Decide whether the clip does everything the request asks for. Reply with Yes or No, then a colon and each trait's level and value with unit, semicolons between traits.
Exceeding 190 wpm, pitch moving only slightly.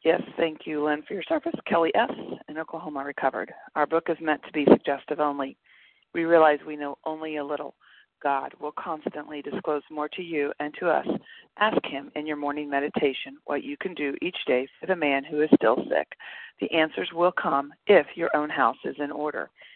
Yes: fast, 205 wpm; narrow, 1.8 semitones